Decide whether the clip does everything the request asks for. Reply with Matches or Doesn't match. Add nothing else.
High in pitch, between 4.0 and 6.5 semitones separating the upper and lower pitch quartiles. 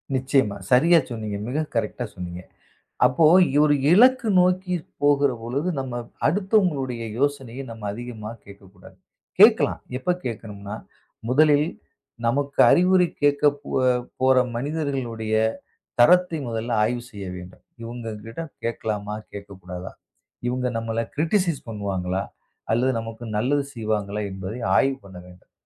Doesn't match